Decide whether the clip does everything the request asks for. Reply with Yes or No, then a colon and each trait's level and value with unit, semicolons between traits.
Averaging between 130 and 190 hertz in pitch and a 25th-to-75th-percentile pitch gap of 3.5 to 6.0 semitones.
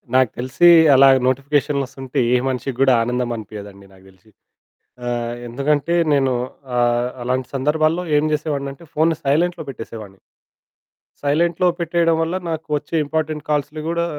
Yes: medium, 140 Hz; average, 4.1 semitones